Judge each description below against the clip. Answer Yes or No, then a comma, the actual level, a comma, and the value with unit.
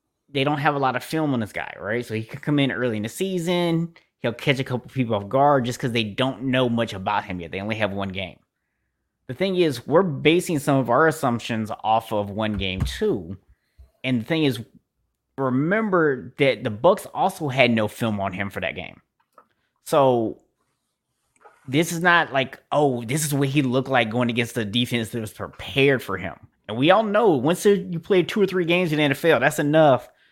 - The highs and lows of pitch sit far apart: Yes, wide, 5.7 semitones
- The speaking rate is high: Yes, fast, 215 wpm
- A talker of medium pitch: No, low, 130 Hz